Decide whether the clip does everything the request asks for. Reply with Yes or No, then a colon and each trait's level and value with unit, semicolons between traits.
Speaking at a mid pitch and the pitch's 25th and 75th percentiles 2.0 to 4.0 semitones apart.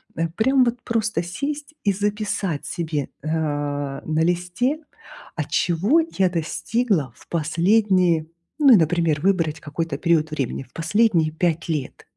No: medium, 170 Hz; average, 5.1 semitones